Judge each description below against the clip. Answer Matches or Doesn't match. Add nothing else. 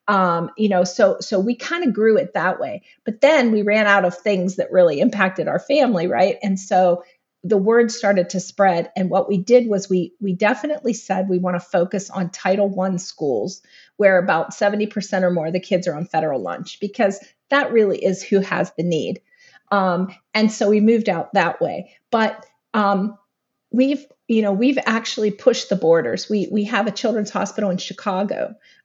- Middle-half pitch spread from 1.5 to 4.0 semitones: Matches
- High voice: Matches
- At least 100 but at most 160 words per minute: Doesn't match